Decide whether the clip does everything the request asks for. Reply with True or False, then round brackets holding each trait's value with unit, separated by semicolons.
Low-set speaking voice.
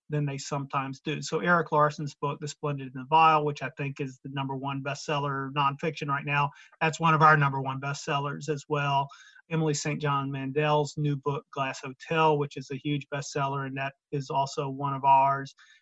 False (145 Hz)